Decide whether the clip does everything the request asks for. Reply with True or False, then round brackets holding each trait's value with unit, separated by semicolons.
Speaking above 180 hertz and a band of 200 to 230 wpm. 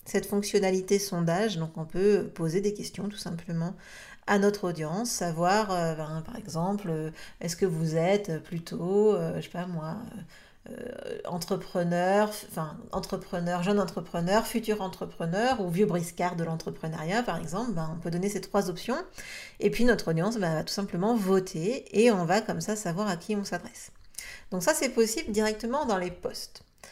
False (190 Hz; 170 wpm)